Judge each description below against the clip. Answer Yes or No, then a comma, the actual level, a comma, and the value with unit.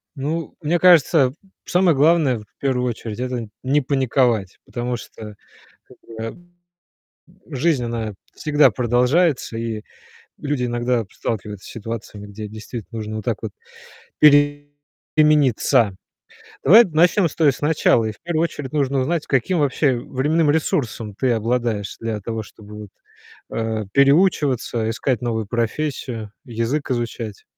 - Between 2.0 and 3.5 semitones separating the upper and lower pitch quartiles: No, average, 4.7 semitones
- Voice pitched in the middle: No, low, 125 Hz